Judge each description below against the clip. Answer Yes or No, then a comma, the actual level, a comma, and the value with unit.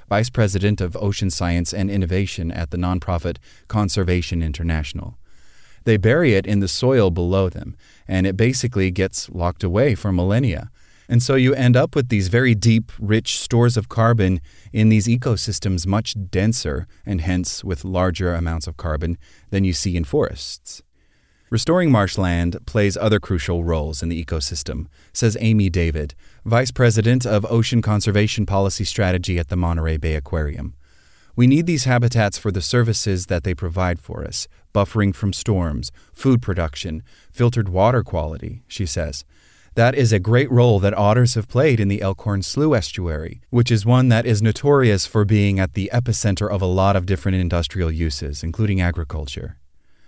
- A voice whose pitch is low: Yes, very low, 95 Hz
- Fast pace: No, average, 165 wpm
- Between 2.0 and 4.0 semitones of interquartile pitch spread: No, average, 4.6 semitones